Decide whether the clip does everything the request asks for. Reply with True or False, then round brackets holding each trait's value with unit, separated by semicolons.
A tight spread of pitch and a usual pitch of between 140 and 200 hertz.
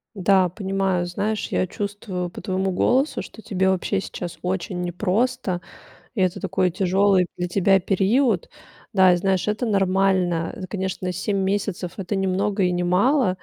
True (1.9 semitones; 190 Hz)